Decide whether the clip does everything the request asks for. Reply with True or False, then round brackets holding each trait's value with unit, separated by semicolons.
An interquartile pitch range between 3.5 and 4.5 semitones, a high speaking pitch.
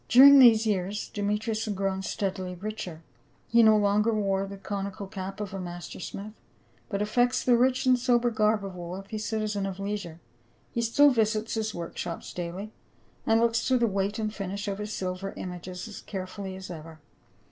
False (2.6 semitones; 205 Hz)